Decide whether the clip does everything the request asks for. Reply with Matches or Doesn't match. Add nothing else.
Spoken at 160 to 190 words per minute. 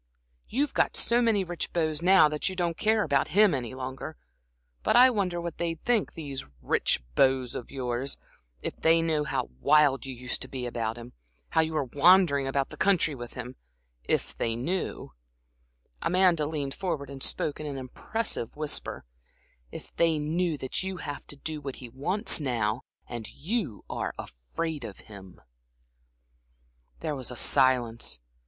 Matches